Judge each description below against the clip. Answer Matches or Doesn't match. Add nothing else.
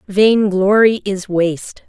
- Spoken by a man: Doesn't match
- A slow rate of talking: Matches